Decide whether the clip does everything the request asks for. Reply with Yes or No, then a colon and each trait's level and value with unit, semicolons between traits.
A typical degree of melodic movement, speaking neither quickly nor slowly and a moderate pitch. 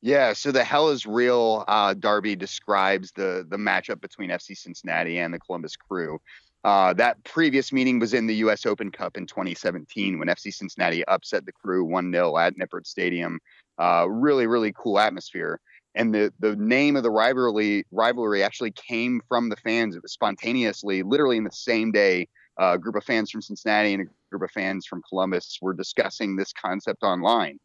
No: average, 3.4 semitones; average, 185 wpm; low, 105 Hz